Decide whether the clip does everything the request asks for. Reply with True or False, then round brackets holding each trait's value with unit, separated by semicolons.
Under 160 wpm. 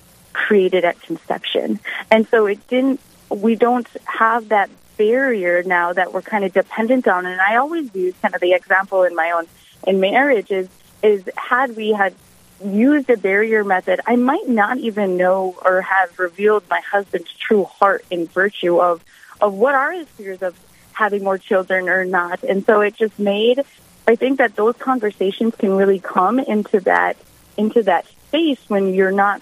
False (180 wpm)